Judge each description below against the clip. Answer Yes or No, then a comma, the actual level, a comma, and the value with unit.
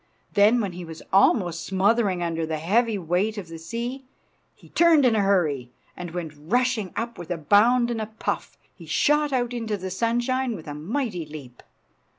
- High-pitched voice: Yes, high, 205 Hz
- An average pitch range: No, wide, 5.9 semitones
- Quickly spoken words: No, average, 185 wpm